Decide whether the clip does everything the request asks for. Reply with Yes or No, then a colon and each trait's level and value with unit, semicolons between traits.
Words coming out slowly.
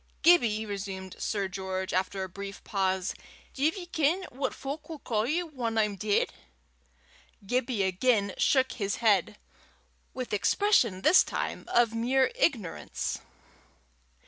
Yes: slow, 125 wpm